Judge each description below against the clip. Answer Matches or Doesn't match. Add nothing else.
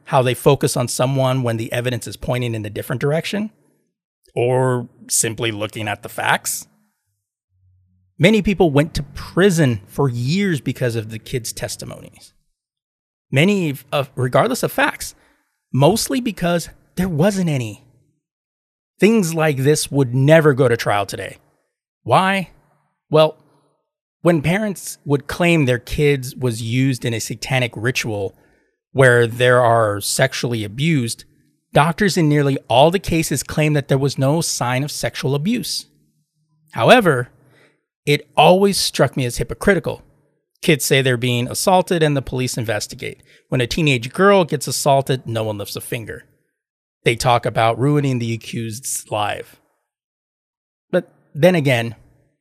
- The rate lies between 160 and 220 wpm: Doesn't match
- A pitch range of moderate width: Matches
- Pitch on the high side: Doesn't match